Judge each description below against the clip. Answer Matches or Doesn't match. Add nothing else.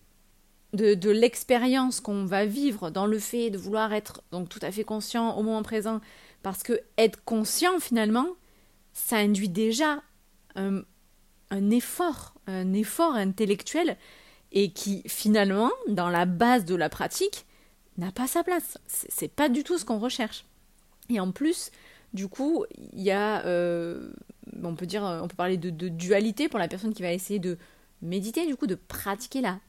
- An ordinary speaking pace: Matches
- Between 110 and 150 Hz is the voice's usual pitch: Doesn't match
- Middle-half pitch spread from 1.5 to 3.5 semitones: Doesn't match